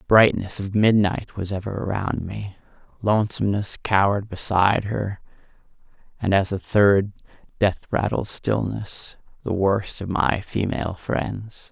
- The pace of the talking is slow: Yes, slow, 125 wpm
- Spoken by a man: Yes, male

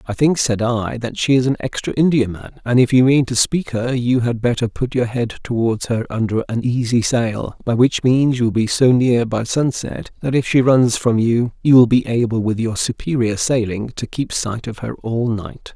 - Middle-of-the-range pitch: No, low, 120 Hz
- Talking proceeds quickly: Yes, fast, 230 wpm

